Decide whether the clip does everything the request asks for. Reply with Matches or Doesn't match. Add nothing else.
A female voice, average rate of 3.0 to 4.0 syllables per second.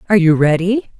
Doesn't match